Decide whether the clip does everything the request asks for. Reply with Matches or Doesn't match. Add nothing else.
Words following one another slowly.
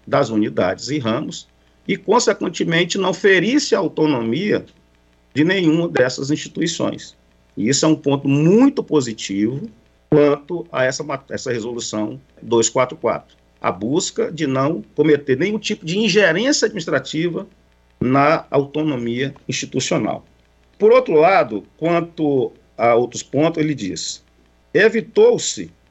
Matches